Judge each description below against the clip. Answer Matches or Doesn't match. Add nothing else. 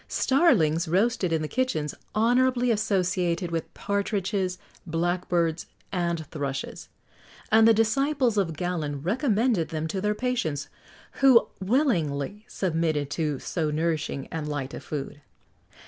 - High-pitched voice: Doesn't match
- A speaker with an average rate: Doesn't match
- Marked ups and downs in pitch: Matches